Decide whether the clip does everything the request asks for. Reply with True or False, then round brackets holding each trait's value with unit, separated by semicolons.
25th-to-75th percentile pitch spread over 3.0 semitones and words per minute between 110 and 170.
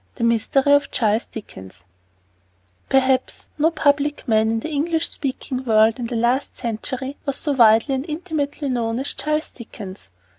True (4.1 semitones; 155 wpm)